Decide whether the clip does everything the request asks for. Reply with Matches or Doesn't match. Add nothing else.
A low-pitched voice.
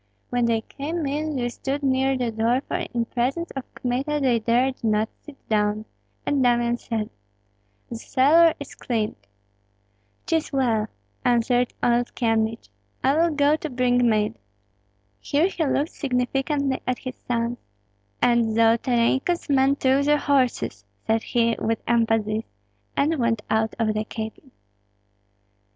Doesn't match